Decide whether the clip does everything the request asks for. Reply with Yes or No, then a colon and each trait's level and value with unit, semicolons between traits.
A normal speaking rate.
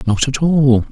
Yes: average, 195 wpm